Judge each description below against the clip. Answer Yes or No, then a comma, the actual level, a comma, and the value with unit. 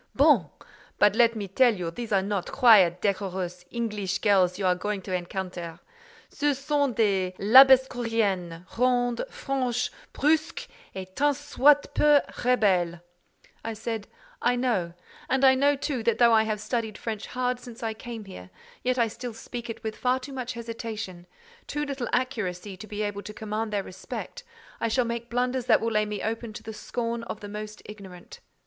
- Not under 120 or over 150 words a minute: No, average, 175 wpm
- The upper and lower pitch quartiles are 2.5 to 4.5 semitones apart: Yes, average, 4.0 semitones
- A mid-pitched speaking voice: No, high, 225 Hz